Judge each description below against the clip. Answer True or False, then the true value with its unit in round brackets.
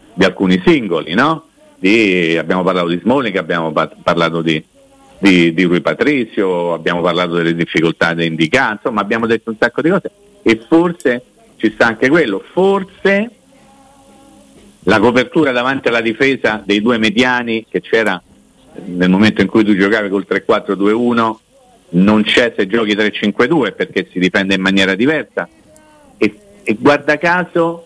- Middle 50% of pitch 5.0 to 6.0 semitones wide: True (5.6 semitones)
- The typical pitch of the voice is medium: False (105 Hz)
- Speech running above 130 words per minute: True (150 wpm)